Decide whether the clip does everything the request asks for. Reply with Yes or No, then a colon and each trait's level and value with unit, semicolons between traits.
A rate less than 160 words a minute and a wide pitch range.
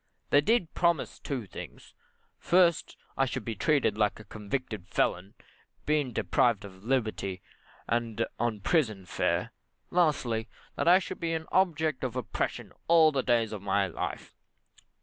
Yes: average, 150 wpm; wide, 6.7 semitones